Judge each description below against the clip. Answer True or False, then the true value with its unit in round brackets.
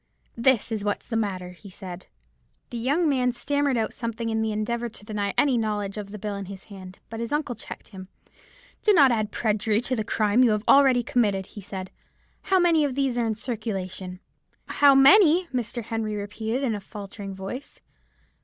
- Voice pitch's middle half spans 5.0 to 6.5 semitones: False (3.8 semitones)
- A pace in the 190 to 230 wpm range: True (195 wpm)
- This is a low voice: False (220 Hz)